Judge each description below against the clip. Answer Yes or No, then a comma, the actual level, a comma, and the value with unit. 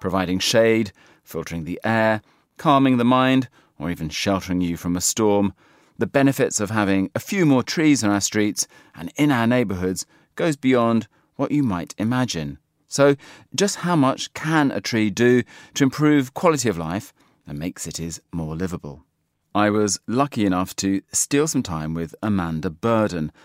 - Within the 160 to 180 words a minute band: Yes, average, 165 wpm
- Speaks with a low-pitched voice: Yes, low, 110 Hz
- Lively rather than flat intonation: Yes, wide, 6.1 semitones